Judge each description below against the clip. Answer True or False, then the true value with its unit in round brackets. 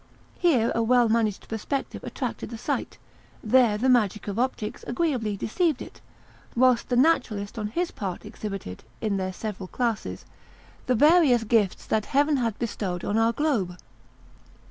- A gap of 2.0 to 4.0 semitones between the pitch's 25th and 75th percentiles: True (3.6 semitones)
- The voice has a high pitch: True (230 Hz)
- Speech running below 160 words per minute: True (150 wpm)